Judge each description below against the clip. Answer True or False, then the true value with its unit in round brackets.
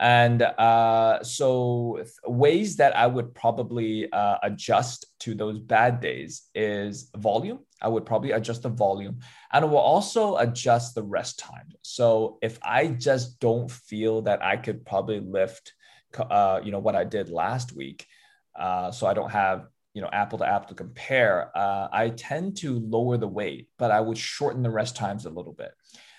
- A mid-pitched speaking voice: False (115 Hz)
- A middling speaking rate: True (180 wpm)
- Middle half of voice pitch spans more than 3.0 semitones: False (2.4 semitones)